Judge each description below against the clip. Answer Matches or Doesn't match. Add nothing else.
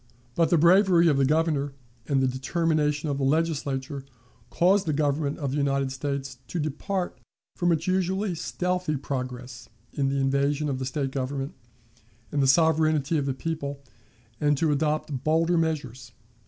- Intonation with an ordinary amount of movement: Matches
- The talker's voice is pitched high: Doesn't match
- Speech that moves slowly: Doesn't match